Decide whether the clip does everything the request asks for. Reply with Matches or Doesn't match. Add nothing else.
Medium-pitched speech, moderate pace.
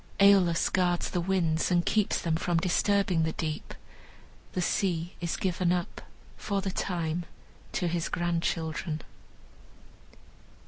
Doesn't match